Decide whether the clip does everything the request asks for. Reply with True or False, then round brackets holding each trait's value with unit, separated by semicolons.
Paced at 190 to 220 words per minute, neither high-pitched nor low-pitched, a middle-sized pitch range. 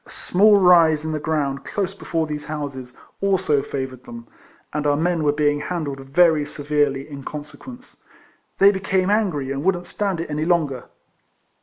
False (165 wpm; 155 Hz; 3.8 semitones)